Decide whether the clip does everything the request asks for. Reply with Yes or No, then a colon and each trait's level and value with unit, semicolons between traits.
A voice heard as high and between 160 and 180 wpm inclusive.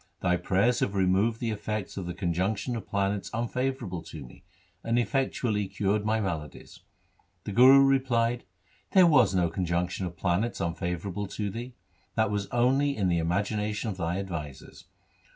No: low, 100 Hz; average, 165 wpm